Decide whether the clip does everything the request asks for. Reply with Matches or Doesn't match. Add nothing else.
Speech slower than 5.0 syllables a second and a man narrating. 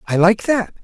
Matches